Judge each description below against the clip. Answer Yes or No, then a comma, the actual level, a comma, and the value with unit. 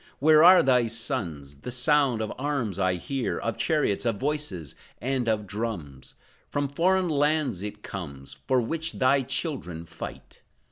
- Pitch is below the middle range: Yes, low, 125 Hz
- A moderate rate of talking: Yes, average, 150 wpm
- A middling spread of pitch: No, wide, 6.7 semitones